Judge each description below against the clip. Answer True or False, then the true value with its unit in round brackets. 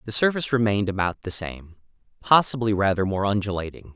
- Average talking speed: True (150 wpm)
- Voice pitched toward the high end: False (105 Hz)